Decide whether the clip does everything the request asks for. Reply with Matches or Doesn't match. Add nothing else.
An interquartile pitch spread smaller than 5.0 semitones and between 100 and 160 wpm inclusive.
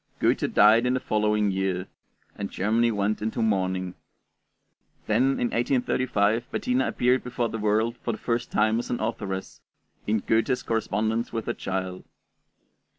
Matches